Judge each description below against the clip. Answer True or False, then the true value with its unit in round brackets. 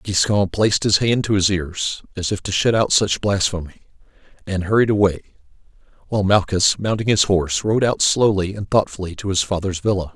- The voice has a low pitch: True (100 Hz)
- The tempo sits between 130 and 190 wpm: True (185 wpm)